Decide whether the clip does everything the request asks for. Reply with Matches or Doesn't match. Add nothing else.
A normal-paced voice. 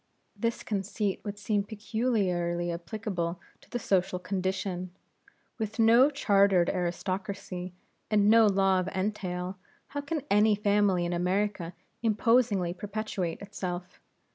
Doesn't match